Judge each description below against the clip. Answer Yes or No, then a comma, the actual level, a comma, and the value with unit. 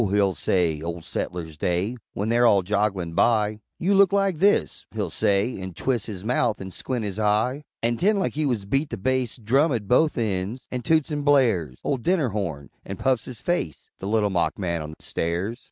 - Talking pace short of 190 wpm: No, fast, 205 wpm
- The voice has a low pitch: Yes, low, 110 Hz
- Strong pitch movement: Yes, wide, 5.7 semitones